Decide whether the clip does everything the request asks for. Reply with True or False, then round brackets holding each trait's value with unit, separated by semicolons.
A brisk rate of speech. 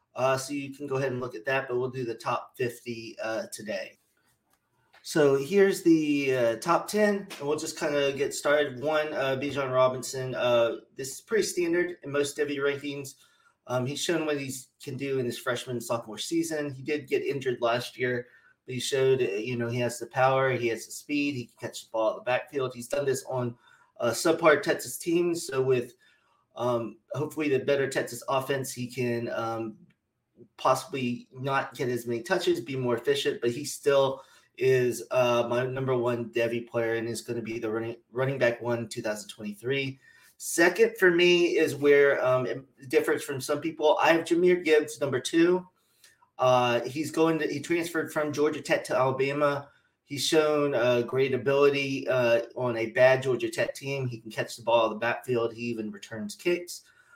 False (195 wpm)